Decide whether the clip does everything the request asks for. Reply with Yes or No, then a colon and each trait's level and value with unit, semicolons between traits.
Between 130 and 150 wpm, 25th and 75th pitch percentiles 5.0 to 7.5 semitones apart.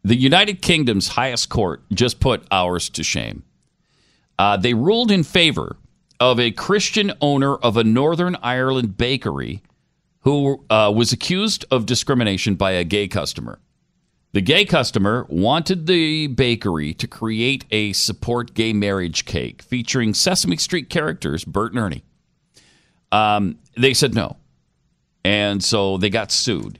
Yes: average, 140 wpm; wide, 5.4 semitones